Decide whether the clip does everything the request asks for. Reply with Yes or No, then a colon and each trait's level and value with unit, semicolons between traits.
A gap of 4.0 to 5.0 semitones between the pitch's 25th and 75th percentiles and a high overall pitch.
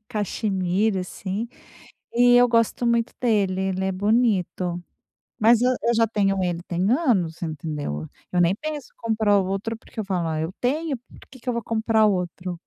Yes: average, 4.3 semitones; high, 205 Hz